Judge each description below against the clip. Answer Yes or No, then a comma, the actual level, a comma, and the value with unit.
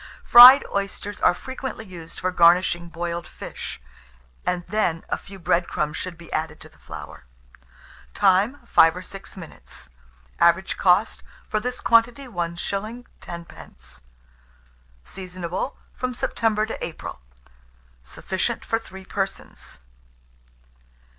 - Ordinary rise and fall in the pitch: Yes, average, 4.3 semitones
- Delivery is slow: Yes, slow, 120 wpm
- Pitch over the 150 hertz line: Yes, medium, 185 Hz